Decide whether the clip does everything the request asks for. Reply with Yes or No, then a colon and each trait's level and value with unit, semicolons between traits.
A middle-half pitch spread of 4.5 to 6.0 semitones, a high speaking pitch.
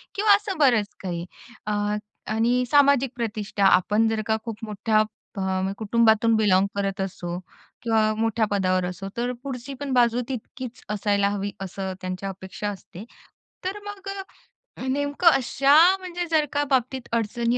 Yes: average, 4.8 semitones; high, 225 Hz